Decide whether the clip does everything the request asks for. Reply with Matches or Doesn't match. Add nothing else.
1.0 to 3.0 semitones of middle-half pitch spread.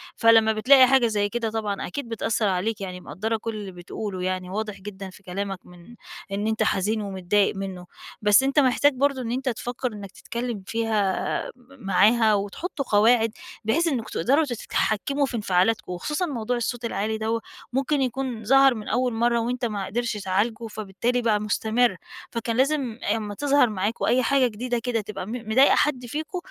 Doesn't match